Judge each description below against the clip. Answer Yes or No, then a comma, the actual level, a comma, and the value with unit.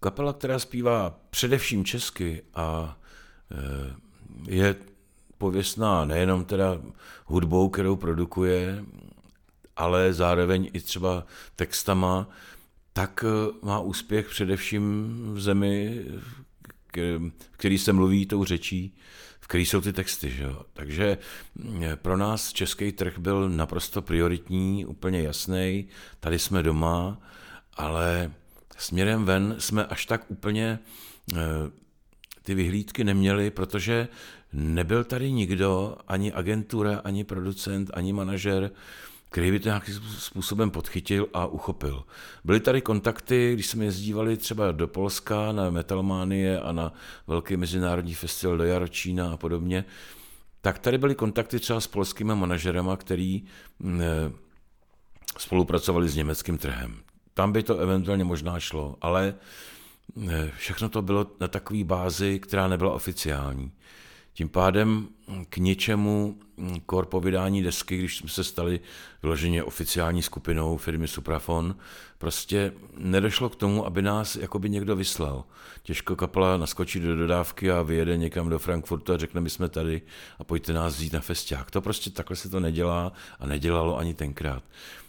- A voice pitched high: No, very low, 95 Hz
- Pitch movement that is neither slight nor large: Yes, average, 3.0 semitones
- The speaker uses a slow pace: No, average, 130 wpm